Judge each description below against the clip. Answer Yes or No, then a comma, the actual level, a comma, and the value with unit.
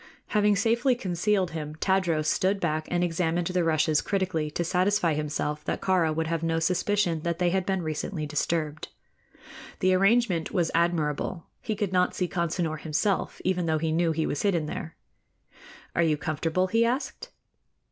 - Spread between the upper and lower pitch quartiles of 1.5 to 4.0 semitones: Yes, average, 3.0 semitones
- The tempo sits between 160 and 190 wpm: Yes, average, 165 wpm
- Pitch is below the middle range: No, medium, 170 Hz